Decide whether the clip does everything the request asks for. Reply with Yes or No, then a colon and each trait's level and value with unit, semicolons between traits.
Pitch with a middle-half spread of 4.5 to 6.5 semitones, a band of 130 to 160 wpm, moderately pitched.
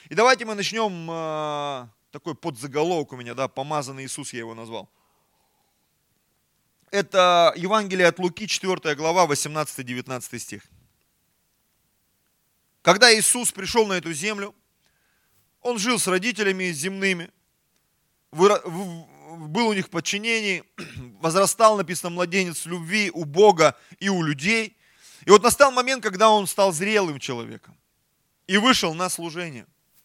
No: average, 5.2 semitones; average, 120 wpm; medium, 180 Hz